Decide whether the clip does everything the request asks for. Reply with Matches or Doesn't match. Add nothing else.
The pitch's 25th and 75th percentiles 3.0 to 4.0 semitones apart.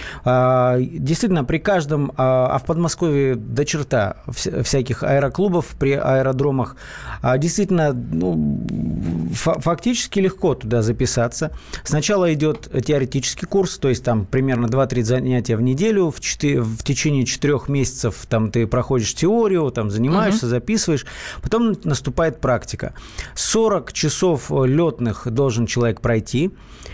Doesn't match